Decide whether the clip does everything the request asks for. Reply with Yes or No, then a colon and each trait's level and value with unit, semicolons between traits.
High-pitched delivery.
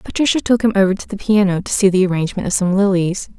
Yes: high, 195 Hz